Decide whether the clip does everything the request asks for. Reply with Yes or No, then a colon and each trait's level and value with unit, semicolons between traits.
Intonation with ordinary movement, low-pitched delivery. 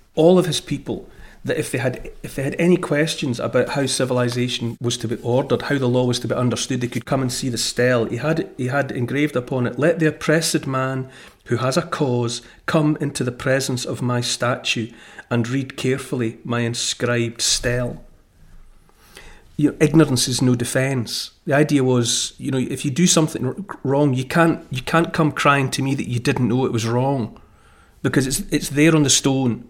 Yes: average, 3.1 semitones; low, 130 Hz